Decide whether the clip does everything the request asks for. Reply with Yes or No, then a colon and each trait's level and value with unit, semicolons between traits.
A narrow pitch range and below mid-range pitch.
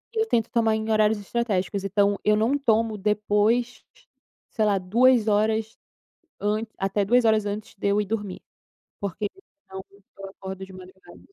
No: narrow, 2.1 semitones; high, 210 Hz